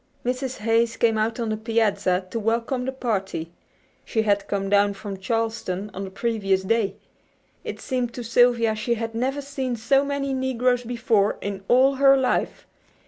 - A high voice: Yes, high, 230 Hz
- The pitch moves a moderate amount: Yes, average, 3.7 semitones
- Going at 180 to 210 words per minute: No, average, 170 wpm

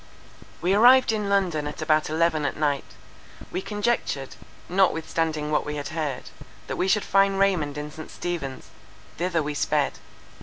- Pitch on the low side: No, medium, 160 Hz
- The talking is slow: No, average, 155 wpm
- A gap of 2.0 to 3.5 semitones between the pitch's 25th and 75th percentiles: No, average, 4.6 semitones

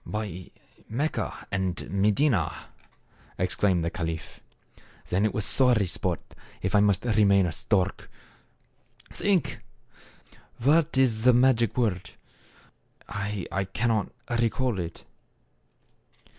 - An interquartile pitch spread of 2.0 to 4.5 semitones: Yes, average, 4.2 semitones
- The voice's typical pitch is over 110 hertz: No, low, 105 Hz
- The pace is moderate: No, slow, 115 wpm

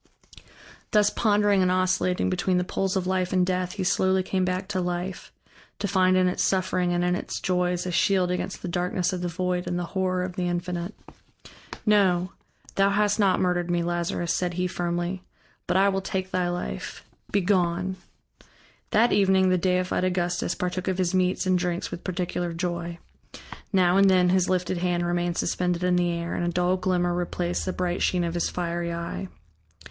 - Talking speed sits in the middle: Yes, average, 190 wpm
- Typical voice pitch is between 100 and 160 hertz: No, medium, 180 Hz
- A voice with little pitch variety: Yes, narrow, 1.1 semitones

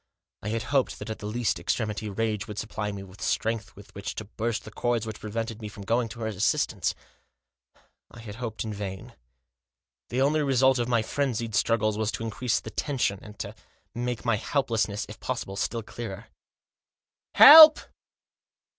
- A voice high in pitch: No, low, 110 Hz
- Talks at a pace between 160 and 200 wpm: Yes, average, 180 wpm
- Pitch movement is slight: Yes, narrow, 2.3 semitones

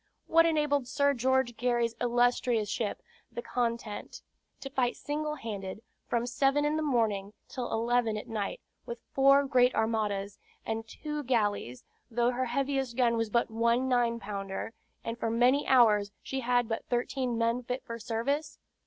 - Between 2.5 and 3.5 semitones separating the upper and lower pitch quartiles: Yes, average, 2.8 semitones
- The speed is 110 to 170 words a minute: Yes, average, 160 wpm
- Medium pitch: No, high, 240 Hz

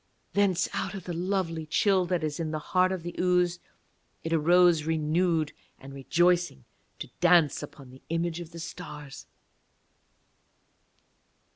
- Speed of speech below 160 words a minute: Yes, average, 140 wpm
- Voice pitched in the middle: Yes, medium, 170 Hz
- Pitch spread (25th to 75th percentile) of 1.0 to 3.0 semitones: Yes, narrow, 2.5 semitones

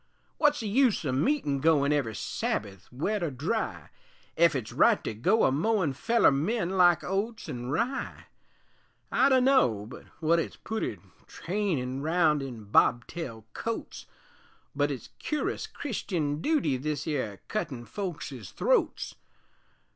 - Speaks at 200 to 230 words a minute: No, slow, 135 wpm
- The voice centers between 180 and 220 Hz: No, medium, 160 Hz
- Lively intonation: Yes, wide, 8.6 semitones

